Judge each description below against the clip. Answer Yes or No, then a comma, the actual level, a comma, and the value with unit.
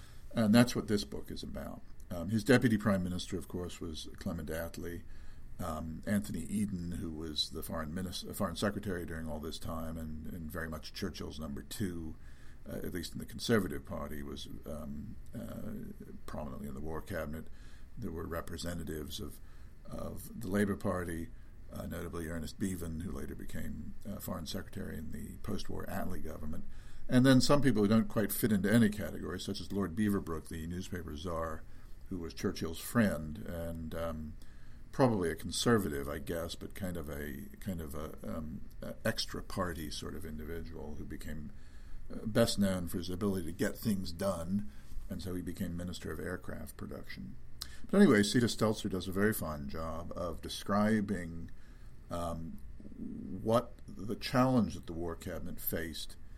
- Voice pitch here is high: No, very low, 85 Hz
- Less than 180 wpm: Yes, average, 170 wpm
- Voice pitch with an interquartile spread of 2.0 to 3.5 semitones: No, average, 4.1 semitones